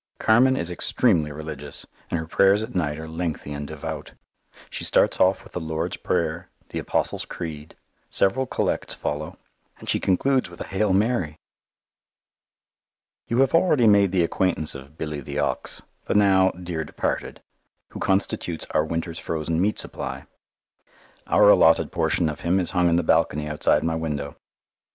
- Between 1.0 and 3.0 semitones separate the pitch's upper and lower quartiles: No, average, 3.8 semitones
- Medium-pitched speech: No, very low, 85 Hz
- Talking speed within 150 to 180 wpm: Yes, average, 160 wpm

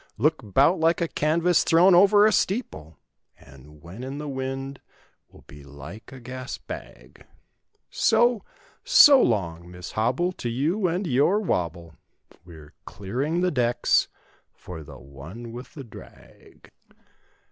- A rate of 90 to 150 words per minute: Yes, average, 140 wpm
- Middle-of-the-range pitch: No, low, 130 Hz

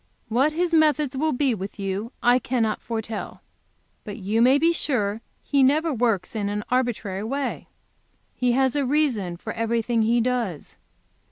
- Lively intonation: No, average, 4.3 semitones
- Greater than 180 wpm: No, average, 165 wpm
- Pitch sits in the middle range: No, high, 240 Hz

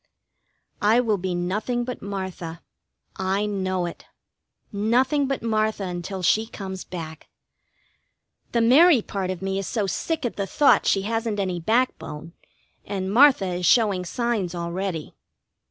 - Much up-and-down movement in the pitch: No, average, 3.9 semitones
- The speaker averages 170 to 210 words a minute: No, average, 140 wpm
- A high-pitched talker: Yes, high, 200 Hz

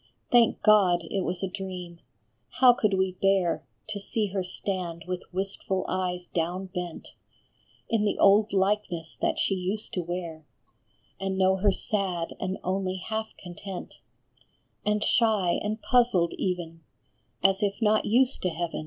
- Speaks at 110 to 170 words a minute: Yes, average, 150 wpm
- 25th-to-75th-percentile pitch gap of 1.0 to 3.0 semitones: Yes, narrow, 2.6 semitones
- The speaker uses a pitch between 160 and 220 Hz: Yes, high, 190 Hz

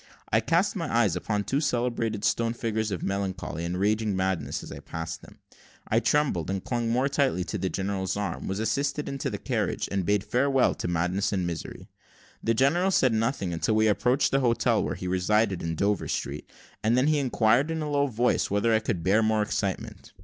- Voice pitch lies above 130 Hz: No, low, 110 Hz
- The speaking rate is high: Yes, fast, 210 wpm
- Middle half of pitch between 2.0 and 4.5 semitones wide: No, average, 4.9 semitones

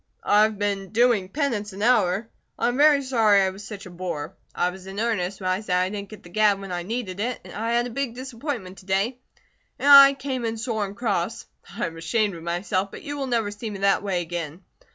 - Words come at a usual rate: No, fast, 240 wpm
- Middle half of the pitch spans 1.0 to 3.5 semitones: No, average, 4.0 semitones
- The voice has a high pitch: Yes, high, 205 Hz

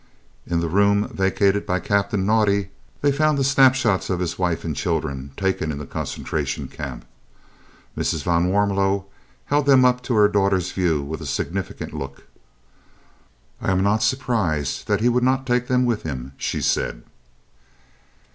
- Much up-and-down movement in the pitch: Yes, wide, 6.3 semitones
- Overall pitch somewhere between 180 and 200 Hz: No, low, 100 Hz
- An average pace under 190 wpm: Yes, average, 160 wpm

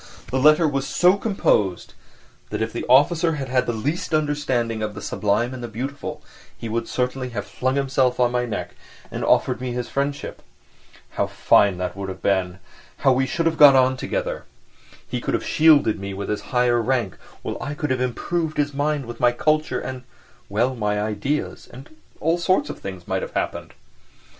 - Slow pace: No, average, 195 wpm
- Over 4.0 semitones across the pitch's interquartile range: Yes, average, 4.7 semitones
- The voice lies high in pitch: No, low, 130 Hz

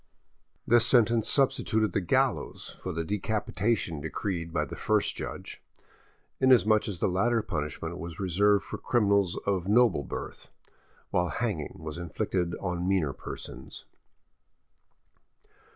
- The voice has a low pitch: Yes, very low, 95 Hz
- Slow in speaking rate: Yes, slow, 120 wpm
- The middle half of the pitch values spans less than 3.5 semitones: No, average, 4.3 semitones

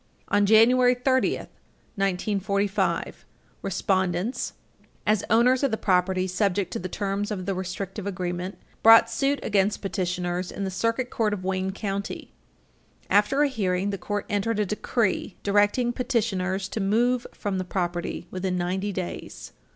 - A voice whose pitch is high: Yes, high, 200 Hz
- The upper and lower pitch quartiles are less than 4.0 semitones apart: Yes, average, 2.9 semitones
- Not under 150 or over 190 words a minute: No, average, 140 wpm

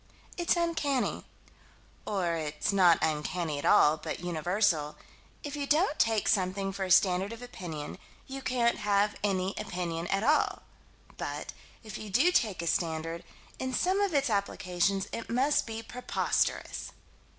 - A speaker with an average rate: Yes, average, 150 wpm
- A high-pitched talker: Yes, high, 200 Hz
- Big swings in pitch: Yes, wide, 6.2 semitones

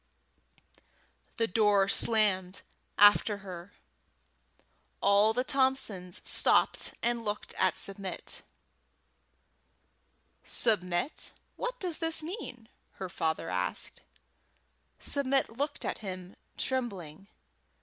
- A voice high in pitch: Yes, high, 205 Hz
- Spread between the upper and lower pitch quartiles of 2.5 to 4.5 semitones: No, average, 5.3 semitones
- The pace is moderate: No, slow, 90 wpm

